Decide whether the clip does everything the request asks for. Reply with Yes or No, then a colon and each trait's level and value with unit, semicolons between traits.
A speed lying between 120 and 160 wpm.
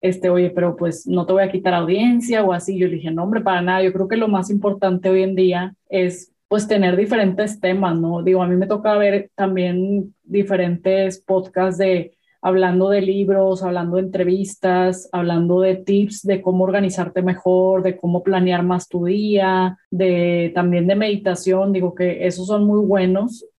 No: average, 185 wpm